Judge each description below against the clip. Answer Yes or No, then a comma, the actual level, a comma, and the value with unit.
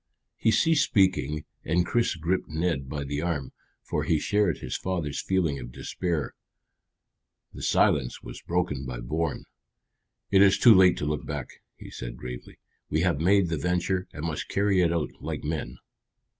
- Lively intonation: No, average, 4.3 semitones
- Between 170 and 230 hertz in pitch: No, very low, 80 Hz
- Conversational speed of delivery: Yes, average, 170 wpm